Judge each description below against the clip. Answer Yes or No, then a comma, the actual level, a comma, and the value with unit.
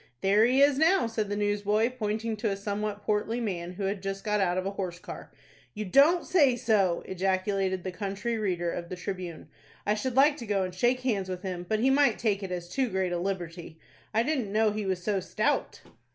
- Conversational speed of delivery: No, fast, 225 wpm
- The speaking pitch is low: No, high, 205 Hz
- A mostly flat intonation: No, average, 3.5 semitones